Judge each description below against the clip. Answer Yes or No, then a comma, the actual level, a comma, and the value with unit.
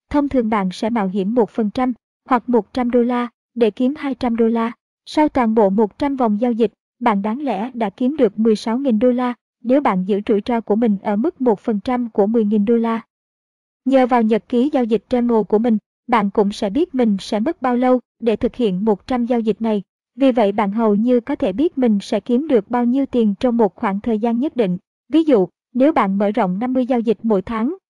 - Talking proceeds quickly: No, average, 225 wpm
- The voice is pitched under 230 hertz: No, high, 235 Hz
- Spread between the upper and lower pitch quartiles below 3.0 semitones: Yes, narrow, 2.6 semitones